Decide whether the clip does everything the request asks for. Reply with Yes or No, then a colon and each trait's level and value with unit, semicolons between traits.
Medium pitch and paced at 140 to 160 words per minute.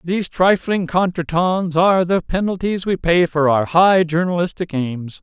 Yes: medium, 175 Hz; average, 150 wpm